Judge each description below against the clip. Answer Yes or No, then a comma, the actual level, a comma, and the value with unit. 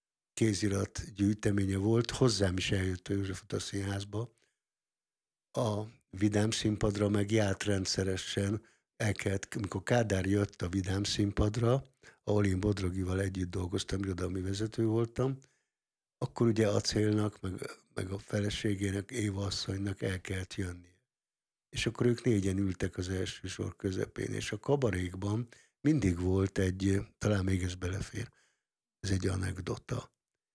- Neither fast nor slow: Yes, average, 130 wpm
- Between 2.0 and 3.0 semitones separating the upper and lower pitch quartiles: Yes, narrow, 2.5 semitones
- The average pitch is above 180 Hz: No, low, 100 Hz